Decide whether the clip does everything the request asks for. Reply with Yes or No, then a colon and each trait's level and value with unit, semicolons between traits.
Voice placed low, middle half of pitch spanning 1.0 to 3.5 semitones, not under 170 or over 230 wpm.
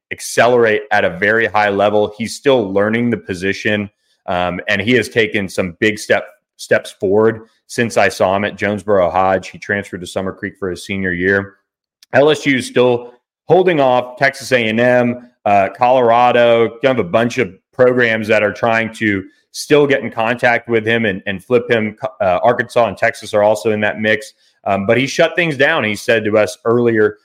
Yes: low, 110 Hz; average, 3.2 semitones; average, 190 wpm